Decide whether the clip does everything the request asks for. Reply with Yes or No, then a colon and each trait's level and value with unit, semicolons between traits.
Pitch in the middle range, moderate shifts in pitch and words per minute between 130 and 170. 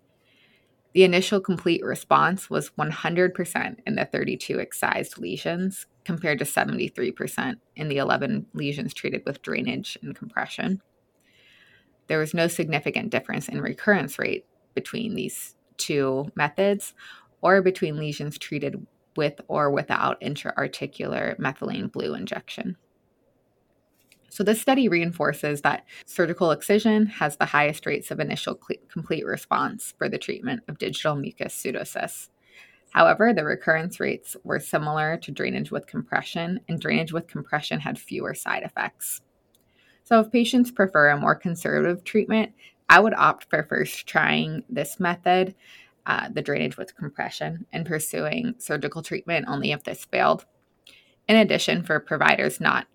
Yes: medium, 175 Hz; average, 4.4 semitones; slow, 135 wpm